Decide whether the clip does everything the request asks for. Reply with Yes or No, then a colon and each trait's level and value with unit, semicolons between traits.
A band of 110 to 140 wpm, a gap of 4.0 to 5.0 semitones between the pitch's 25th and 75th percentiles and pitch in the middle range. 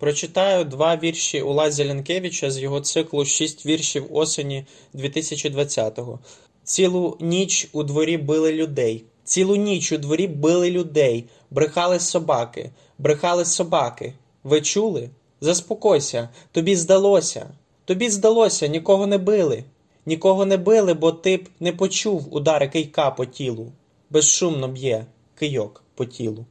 Yes: average, 125 wpm; average, 4.4 semitones; medium, 155 Hz